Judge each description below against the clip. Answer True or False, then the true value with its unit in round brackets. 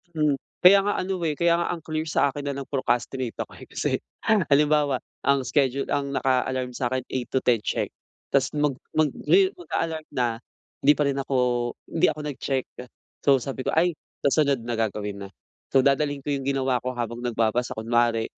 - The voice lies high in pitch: False (135 Hz)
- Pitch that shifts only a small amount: False (3.3 semitones)